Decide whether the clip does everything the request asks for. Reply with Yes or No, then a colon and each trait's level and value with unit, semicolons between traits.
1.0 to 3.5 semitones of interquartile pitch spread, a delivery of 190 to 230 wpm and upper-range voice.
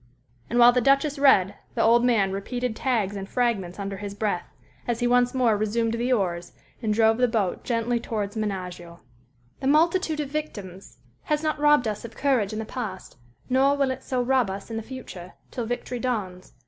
No: average, 4.2 semitones; average, 195 wpm; high, 230 Hz